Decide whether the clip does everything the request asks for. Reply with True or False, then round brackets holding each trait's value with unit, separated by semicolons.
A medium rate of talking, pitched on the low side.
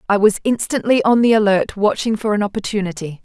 False (185 wpm; 210 Hz)